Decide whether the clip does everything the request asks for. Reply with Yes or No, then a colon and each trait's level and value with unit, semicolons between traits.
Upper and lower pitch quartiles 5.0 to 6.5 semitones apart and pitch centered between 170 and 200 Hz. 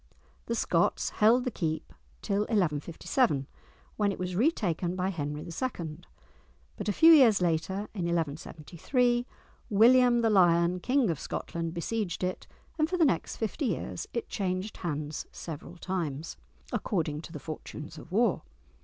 Yes: wide, 5.6 semitones; medium, 185 Hz